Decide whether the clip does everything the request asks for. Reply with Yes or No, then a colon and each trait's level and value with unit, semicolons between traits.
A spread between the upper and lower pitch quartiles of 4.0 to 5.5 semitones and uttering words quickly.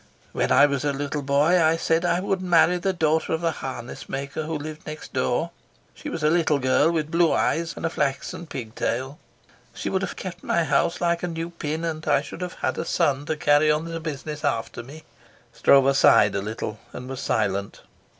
No: average, 3.3 semitones; fast, 210 wpm